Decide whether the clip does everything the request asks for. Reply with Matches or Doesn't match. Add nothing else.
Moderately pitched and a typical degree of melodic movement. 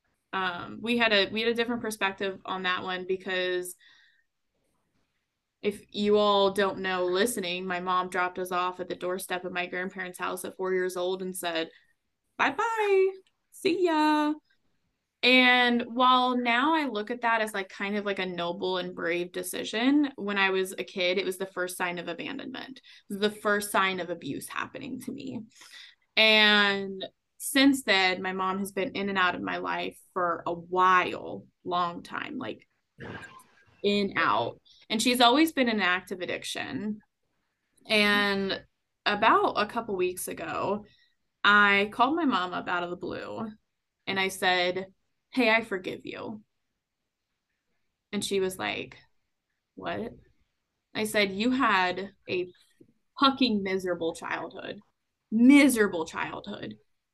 Doesn't match